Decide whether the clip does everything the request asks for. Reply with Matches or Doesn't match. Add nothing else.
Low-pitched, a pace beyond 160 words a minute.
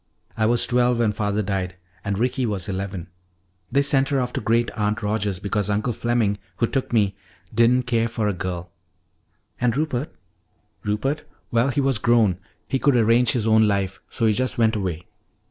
Matches